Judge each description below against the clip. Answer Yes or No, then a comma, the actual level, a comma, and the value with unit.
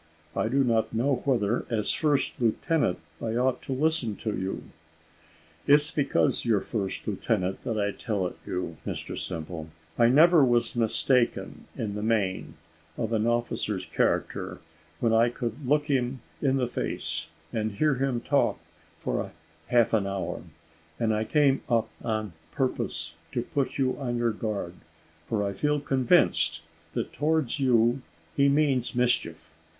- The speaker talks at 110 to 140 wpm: No, average, 150 wpm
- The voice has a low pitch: Yes, low, 120 Hz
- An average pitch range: Yes, average, 4.0 semitones